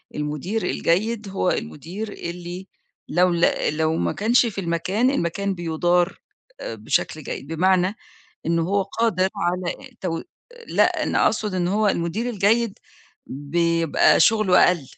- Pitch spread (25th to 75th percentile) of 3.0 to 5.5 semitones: Yes, average, 3.5 semitones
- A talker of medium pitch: Yes, medium, 180 Hz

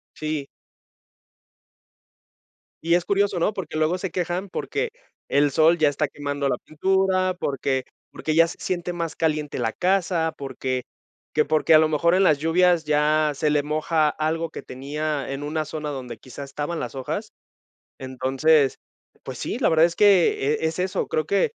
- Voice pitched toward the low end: No, medium, 155 Hz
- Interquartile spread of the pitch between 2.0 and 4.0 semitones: Yes, average, 3.1 semitones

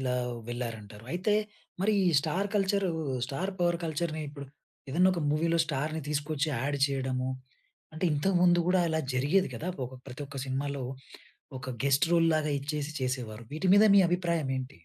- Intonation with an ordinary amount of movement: Yes, average, 4.5 semitones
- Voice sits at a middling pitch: Yes, medium, 150 Hz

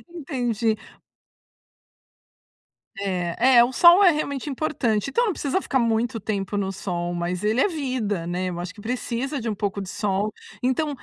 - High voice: Yes, high, 225 Hz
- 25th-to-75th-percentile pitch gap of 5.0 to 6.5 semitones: Yes, wide, 5.6 semitones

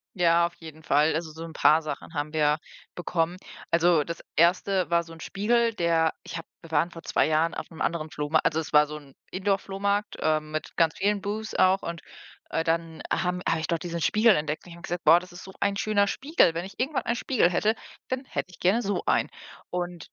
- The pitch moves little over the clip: No, average, 3.4 semitones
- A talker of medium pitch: Yes, medium, 170 Hz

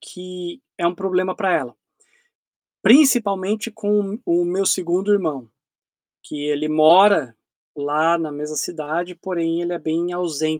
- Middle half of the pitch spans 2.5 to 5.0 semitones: Yes, average, 3.6 semitones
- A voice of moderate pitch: Yes, medium, 175 Hz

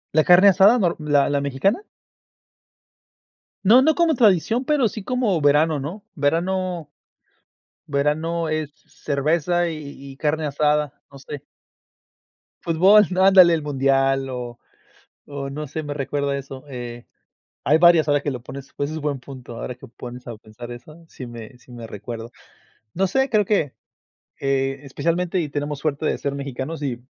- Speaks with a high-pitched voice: No, medium, 150 Hz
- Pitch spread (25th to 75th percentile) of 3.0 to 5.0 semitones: Yes, average, 4.2 semitones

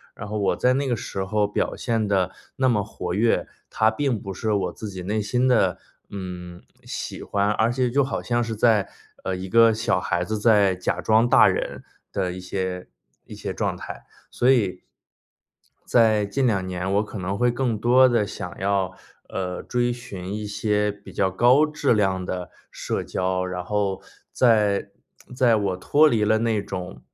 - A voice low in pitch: Yes, low, 105 Hz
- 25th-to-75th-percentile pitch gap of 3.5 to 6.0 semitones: Yes, average, 3.8 semitones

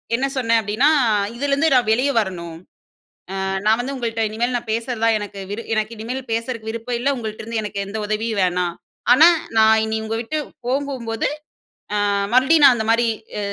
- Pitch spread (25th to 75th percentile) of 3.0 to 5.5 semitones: No, narrow, 2.5 semitones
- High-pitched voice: Yes, high, 230 Hz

